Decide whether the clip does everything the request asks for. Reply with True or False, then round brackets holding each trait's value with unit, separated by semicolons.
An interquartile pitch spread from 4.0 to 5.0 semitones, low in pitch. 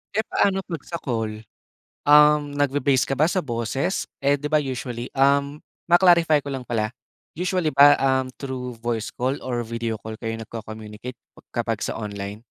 True (4.3 semitones; 130 Hz)